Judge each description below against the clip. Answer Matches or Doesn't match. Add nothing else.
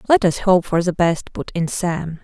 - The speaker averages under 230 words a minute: Doesn't match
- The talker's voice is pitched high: Doesn't match